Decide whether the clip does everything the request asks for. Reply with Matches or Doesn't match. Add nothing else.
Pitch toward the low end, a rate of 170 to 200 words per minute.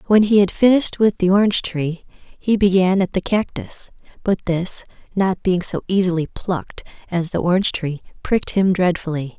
Doesn't match